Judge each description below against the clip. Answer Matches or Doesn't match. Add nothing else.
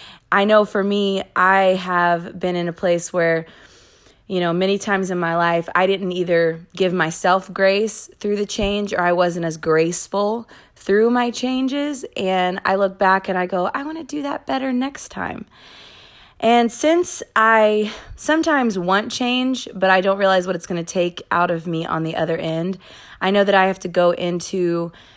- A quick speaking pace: Doesn't match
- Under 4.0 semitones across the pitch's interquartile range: Matches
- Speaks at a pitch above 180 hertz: Matches